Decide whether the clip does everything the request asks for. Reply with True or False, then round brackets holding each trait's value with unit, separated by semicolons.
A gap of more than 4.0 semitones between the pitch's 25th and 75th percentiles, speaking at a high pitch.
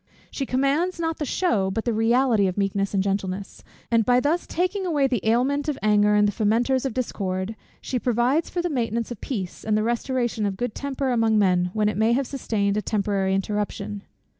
True (4.5 semitones; 225 Hz)